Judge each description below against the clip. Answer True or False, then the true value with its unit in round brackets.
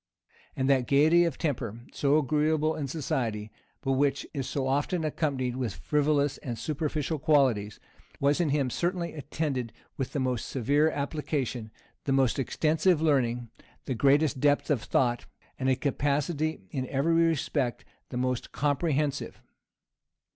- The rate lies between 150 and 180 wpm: False (140 wpm)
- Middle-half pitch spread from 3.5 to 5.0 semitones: False (3.0 semitones)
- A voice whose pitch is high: False (140 Hz)